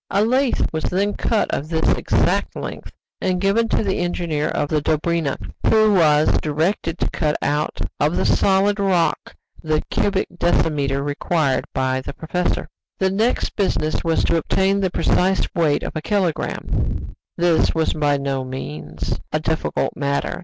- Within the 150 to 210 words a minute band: Yes, average, 160 wpm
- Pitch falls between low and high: Yes, medium, 165 Hz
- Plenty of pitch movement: No, average, 4.4 semitones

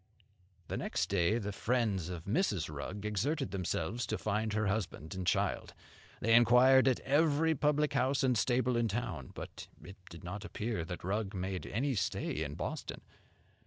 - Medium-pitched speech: No, low, 110 Hz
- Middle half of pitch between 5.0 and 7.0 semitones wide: Yes, average, 5.3 semitones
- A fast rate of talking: No, average, 165 wpm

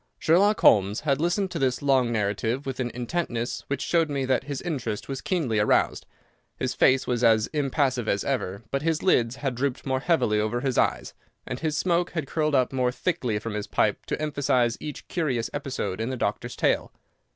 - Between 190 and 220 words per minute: Yes, average, 195 wpm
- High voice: No, low, 130 Hz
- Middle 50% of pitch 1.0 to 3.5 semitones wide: No, average, 4.4 semitones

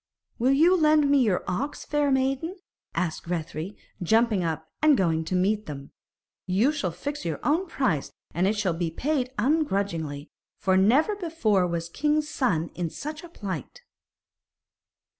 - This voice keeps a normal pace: Yes, average, 155 wpm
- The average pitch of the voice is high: Yes, high, 210 Hz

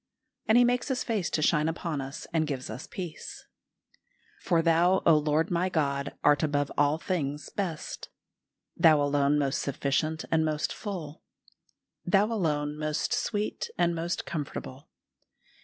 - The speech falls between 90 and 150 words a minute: Yes, average, 145 wpm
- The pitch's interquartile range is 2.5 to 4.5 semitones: Yes, average, 3.1 semitones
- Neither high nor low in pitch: Yes, medium, 155 Hz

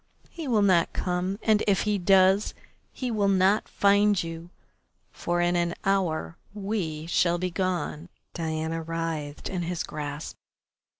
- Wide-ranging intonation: No, average, 3.1 semitones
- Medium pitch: Yes, medium, 180 Hz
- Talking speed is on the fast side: No, average, 140 wpm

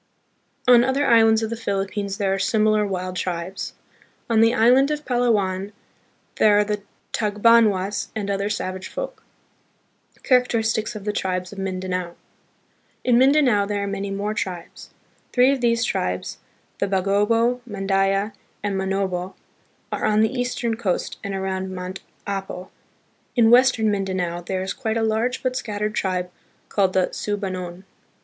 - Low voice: No, high, 205 Hz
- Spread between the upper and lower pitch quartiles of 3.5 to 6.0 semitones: No, average, 3.1 semitones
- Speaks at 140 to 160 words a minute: Yes, average, 155 wpm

